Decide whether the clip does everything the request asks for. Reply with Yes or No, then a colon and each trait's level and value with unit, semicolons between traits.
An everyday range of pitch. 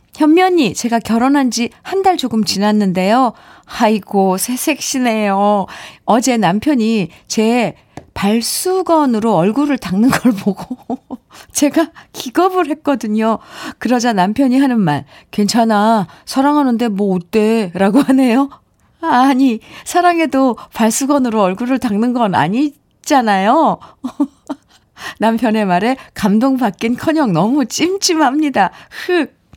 Yes: average, 4.9 semitones